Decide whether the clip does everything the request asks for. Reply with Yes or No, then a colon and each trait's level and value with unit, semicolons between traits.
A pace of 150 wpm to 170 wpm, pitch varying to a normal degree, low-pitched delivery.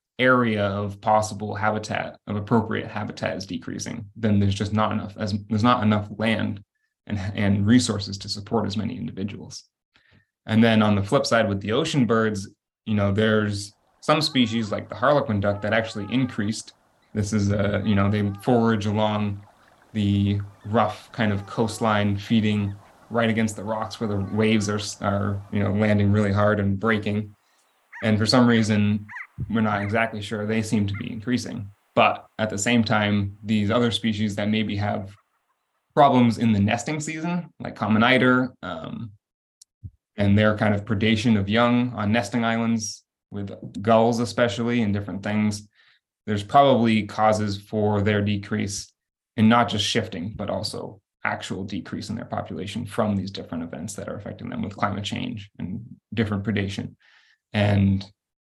No: average, 165 wpm; narrow, 1.9 semitones; low, 105 Hz